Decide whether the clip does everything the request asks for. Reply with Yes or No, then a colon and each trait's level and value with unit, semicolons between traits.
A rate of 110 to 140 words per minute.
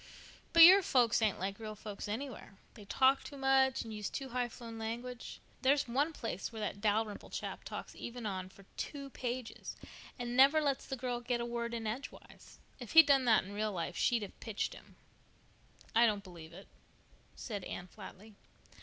No: average, 190 wpm